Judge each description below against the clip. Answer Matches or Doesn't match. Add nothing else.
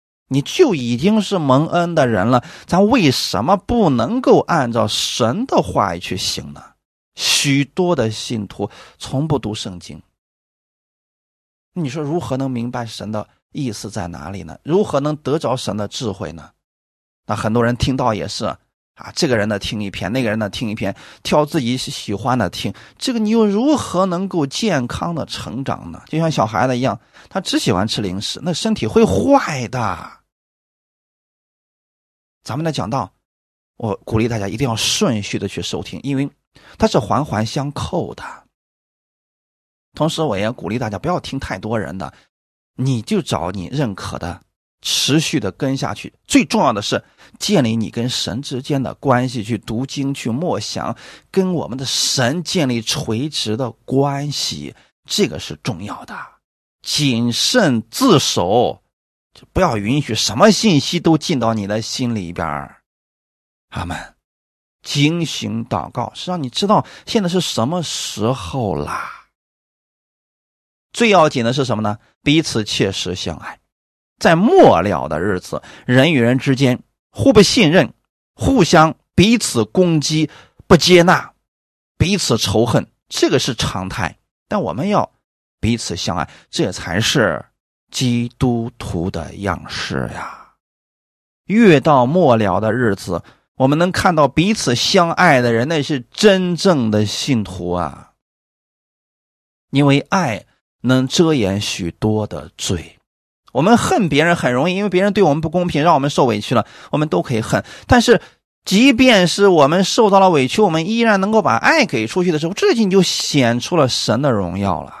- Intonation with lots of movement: Matches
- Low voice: Matches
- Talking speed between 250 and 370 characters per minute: Doesn't match